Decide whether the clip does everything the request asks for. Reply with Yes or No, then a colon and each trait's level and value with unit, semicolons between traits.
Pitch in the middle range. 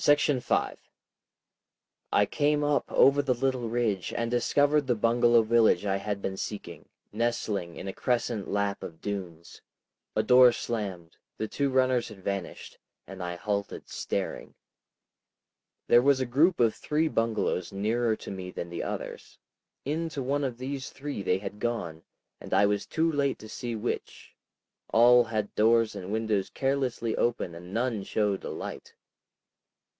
No: low, 115 Hz